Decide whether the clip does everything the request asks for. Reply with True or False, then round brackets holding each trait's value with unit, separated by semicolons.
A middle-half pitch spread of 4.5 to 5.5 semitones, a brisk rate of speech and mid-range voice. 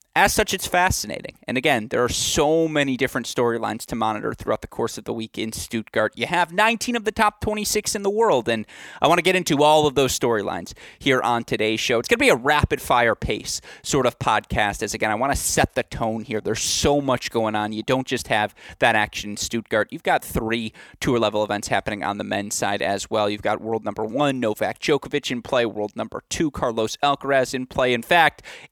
False (5.1 semitones; 230 wpm; 120 Hz)